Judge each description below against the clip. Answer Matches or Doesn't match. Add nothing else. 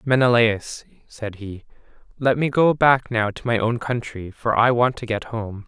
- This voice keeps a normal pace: Matches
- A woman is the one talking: Doesn't match